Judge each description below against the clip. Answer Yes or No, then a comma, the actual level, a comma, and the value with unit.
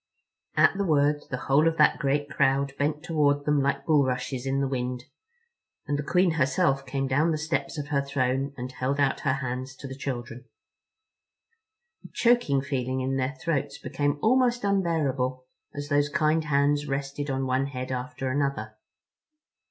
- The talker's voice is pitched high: No, medium, 140 Hz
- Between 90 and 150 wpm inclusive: No, average, 170 wpm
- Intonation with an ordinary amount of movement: No, narrow, 2.1 semitones